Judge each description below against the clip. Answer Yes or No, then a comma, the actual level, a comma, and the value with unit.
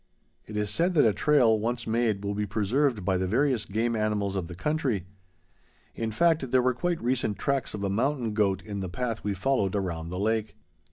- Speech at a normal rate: No, fast, 210 wpm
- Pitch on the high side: No, low, 110 Hz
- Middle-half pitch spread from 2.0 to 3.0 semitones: No, average, 4.1 semitones